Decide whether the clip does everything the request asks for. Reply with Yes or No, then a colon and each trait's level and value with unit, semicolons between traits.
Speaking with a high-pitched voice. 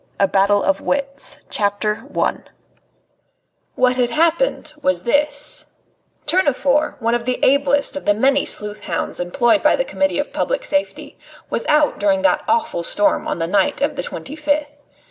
Yes: very high, 280 Hz